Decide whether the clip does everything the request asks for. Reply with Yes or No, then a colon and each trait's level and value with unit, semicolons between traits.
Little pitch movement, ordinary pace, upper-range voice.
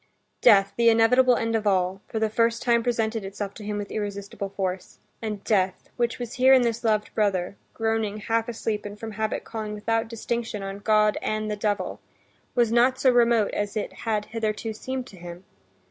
Yes: narrow, 2.2 semitones; average, 190 wpm; high, 220 Hz